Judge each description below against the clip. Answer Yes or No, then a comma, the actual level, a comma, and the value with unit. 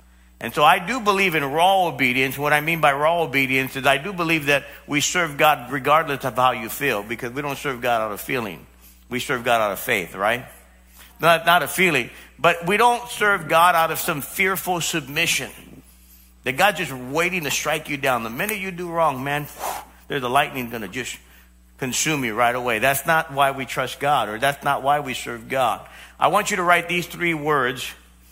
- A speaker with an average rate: No, fast, 215 wpm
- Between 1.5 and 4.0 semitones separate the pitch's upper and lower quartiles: No, average, 5.2 semitones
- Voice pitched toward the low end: No, medium, 145 Hz